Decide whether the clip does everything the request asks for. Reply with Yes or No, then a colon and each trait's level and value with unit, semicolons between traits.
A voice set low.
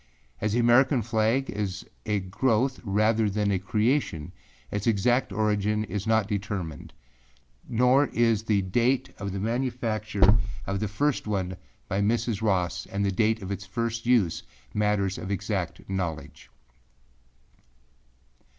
Yes: low, 105 Hz